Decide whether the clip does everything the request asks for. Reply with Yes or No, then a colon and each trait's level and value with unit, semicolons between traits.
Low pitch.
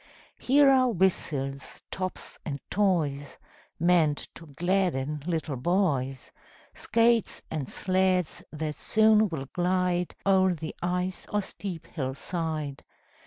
No: medium, 175 Hz